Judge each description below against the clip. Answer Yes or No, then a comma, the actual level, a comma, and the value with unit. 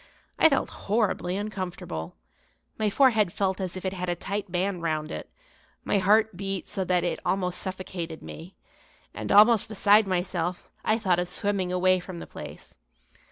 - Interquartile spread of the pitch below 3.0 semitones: Yes, narrow, 2.4 semitones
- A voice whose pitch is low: No, medium, 185 Hz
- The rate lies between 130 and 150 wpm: No, average, 165 wpm